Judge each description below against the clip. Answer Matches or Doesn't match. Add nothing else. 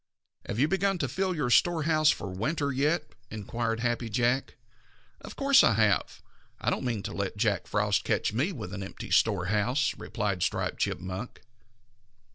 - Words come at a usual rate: Matches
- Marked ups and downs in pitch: Matches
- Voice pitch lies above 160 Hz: Doesn't match